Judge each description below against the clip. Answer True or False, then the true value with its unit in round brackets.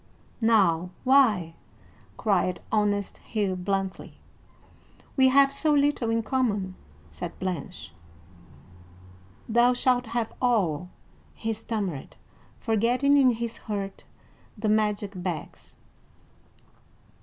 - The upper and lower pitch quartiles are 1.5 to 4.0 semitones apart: False (4.5 semitones)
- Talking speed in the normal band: False (95 wpm)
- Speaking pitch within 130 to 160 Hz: False (215 Hz)